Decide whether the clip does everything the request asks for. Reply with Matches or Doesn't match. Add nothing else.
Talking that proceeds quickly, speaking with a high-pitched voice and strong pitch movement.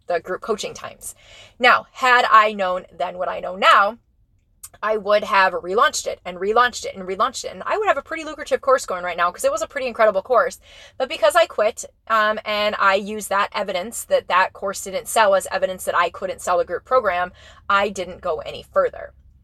Matches